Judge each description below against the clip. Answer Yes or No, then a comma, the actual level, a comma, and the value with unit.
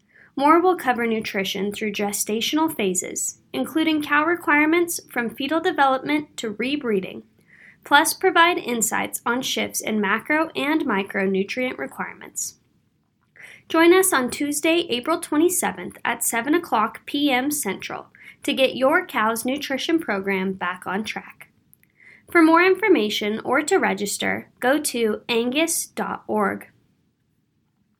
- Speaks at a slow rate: Yes, slow, 115 wpm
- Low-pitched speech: No, very high, 265 Hz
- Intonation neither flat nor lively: No, wide, 6.6 semitones